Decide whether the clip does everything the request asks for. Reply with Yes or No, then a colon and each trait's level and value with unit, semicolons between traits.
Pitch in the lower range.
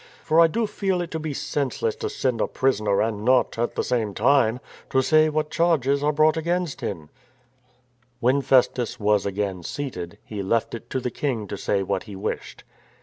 Yes: low, 130 Hz